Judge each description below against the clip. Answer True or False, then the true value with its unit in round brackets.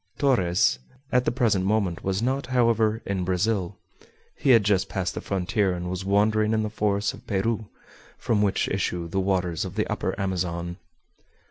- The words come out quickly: False (170 wpm)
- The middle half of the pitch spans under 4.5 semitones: True (3.2 semitones)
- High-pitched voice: False (100 Hz)